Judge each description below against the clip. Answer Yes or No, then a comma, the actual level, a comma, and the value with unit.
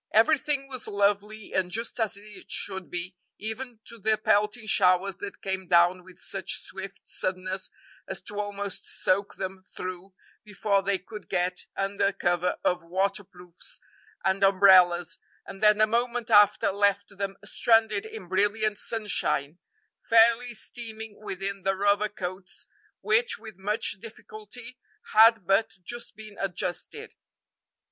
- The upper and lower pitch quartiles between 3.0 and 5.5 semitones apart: No, narrow, 2.6 semitones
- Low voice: No, high, 200 Hz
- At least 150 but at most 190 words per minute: No, slow, 135 wpm